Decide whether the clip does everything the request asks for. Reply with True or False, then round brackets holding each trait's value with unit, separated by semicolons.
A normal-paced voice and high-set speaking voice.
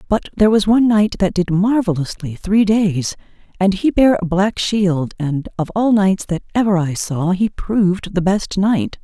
True (190 wpm; 195 Hz)